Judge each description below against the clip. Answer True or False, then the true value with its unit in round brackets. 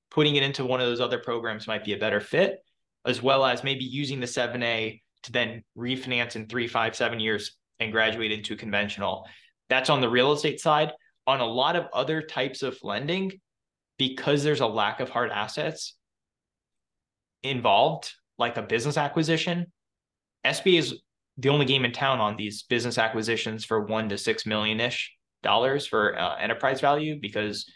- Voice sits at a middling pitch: False (125 Hz)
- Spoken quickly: False (175 wpm)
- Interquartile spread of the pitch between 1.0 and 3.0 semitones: False (4.3 semitones)